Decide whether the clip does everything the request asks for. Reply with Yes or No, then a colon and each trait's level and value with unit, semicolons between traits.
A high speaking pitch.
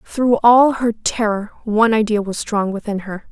Yes: high, 220 Hz